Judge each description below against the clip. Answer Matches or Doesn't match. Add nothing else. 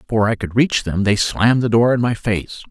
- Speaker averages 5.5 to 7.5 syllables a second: Matches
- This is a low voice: Matches